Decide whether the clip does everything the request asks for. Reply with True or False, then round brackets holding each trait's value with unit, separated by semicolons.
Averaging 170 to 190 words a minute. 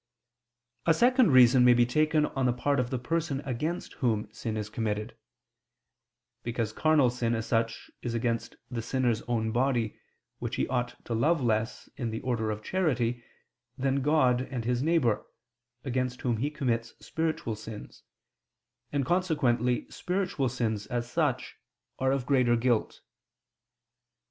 False (150 wpm)